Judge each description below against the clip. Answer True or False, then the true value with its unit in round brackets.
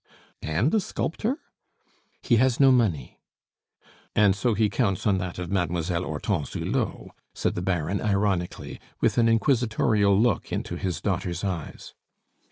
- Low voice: True (100 Hz)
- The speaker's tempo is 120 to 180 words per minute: True (140 wpm)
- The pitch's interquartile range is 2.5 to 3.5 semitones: False (4.5 semitones)